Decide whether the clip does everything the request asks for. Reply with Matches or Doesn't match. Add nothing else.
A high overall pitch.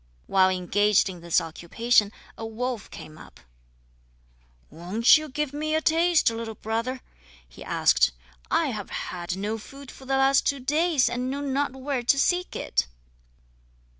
Matches